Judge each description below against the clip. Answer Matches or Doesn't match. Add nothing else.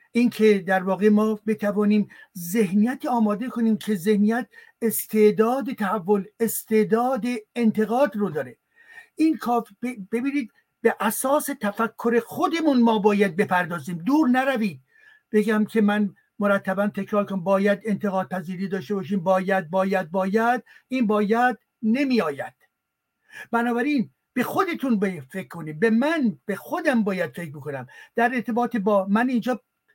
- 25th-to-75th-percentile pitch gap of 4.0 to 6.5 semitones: Doesn't match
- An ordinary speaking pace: Matches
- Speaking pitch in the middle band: Doesn't match